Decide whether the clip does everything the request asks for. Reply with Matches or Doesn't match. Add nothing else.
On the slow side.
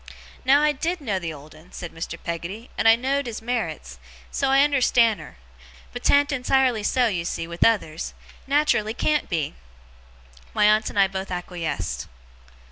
Doesn't match